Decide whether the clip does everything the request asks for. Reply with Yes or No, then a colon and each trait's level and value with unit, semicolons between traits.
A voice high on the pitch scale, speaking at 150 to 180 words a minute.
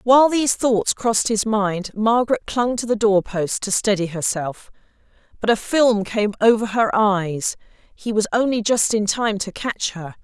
Yes: high, 215 Hz; average, 170 wpm